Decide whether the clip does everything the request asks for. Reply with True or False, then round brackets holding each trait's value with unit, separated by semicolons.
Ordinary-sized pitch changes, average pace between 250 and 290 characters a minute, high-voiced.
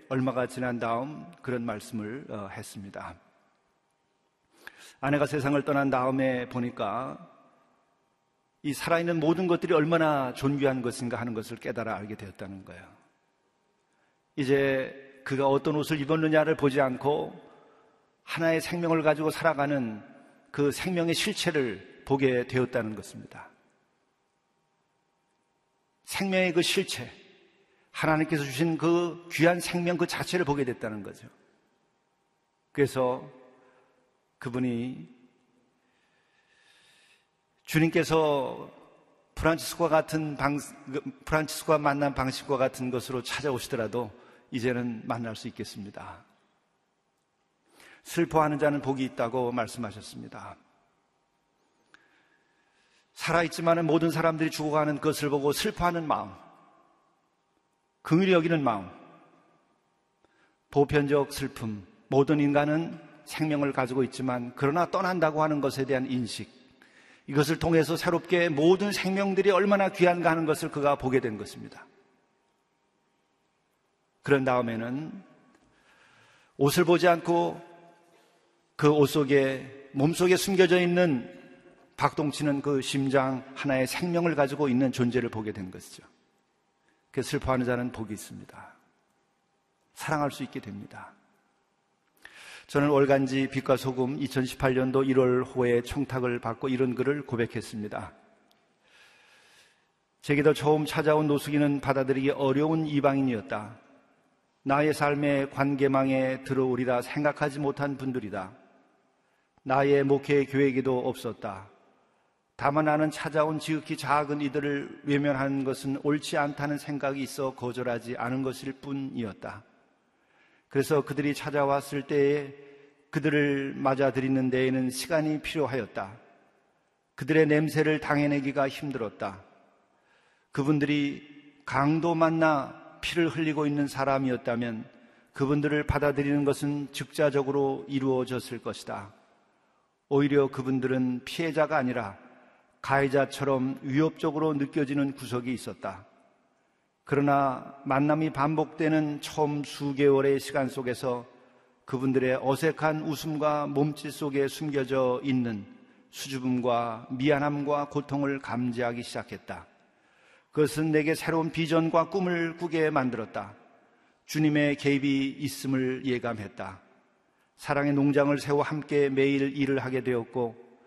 False (3.0 semitones; 265 characters per minute; 140 Hz)